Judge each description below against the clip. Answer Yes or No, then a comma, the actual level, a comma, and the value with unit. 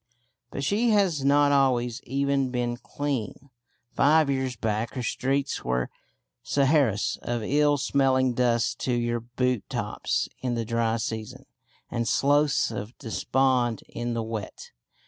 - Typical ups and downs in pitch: Yes, average, 3.0 semitones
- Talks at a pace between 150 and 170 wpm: No, slow, 135 wpm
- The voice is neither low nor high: No, low, 125 Hz